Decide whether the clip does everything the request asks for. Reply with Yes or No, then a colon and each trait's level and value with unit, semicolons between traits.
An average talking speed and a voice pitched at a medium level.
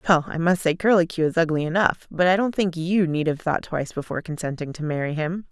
No: fast, 240 wpm; medium, 170 Hz